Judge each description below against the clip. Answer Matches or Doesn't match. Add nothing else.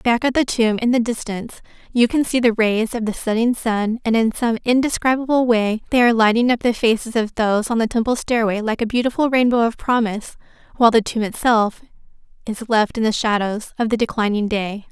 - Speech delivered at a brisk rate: Matches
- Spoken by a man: Doesn't match